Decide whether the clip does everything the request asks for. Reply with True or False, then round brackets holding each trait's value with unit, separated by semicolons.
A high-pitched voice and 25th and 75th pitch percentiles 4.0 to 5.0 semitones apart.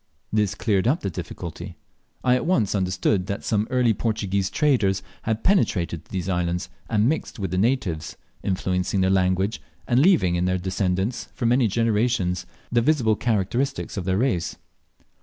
False (100 Hz; 4.4 semitones)